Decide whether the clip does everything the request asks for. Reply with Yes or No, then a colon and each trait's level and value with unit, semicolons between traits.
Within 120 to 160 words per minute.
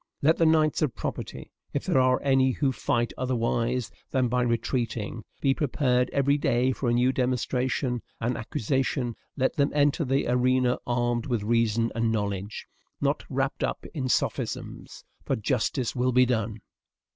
Yes: average, 155 wpm